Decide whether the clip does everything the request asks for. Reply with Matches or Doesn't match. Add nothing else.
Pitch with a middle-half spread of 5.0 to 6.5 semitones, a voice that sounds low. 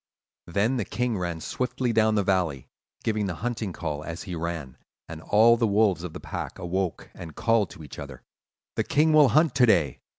Matches